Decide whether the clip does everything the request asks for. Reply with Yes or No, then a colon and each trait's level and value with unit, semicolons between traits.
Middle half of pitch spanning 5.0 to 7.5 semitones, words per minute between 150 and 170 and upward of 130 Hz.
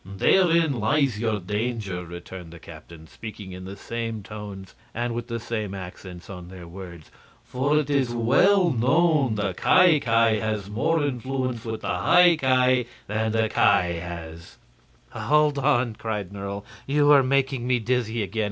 No: average, 5.3 semitones; average, 160 wpm; low, 115 Hz